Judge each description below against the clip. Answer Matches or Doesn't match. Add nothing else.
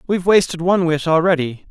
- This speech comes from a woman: Doesn't match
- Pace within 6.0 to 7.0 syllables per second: Matches